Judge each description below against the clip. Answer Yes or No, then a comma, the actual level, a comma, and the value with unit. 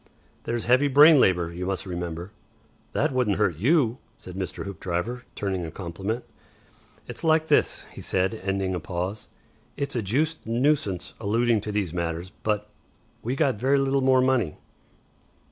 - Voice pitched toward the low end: Yes, low, 105 Hz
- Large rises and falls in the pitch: Yes, wide, 5.9 semitones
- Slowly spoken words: No, average, 155 wpm